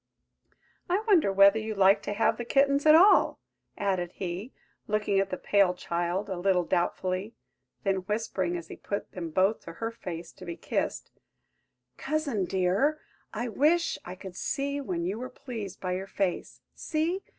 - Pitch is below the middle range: No, high, 200 Hz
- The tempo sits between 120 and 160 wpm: No, average, 170 wpm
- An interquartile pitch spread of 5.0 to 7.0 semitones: Yes, wide, 5.4 semitones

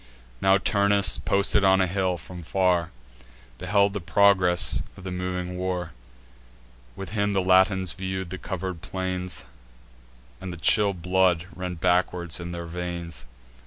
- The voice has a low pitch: Yes, very low, 90 Hz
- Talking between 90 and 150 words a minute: Yes, average, 140 wpm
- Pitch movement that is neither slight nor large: No, narrow, 1.4 semitones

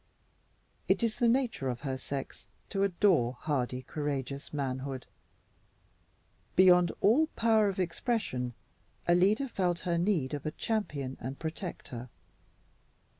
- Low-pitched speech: No, medium, 165 Hz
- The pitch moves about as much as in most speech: No, wide, 7.2 semitones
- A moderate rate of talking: No, slow, 120 wpm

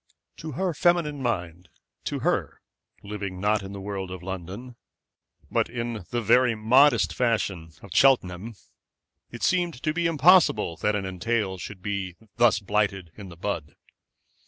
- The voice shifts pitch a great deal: No, average, 4.8 semitones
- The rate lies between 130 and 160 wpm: Yes, average, 150 wpm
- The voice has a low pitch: Yes, low, 105 Hz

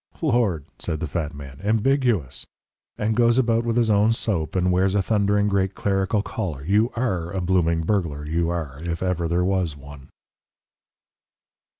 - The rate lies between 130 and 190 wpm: Yes, average, 165 wpm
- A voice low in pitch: Yes, very low, 95 Hz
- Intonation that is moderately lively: Yes, average, 4.6 semitones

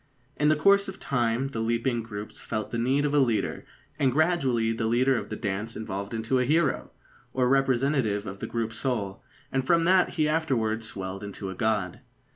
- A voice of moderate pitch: No, low, 120 Hz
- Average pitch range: Yes, average, 3.9 semitones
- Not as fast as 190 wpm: No, average, 195 wpm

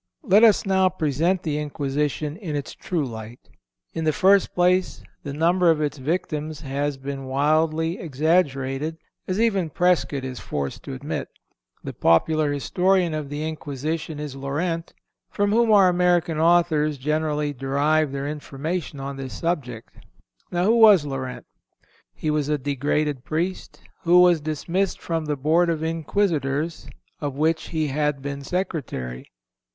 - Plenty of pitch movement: No, average, 3.6 semitones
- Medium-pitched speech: Yes, medium, 155 Hz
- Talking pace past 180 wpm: No, average, 145 wpm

